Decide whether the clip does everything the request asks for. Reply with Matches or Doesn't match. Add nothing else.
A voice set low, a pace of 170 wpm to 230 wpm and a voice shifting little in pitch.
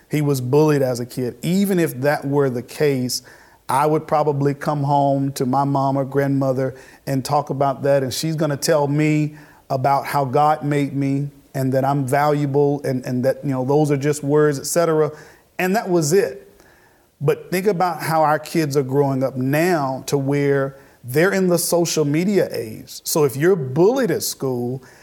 Doesn't match